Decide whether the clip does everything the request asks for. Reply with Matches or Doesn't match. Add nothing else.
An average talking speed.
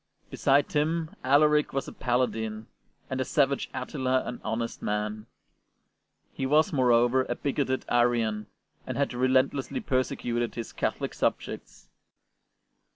Doesn't match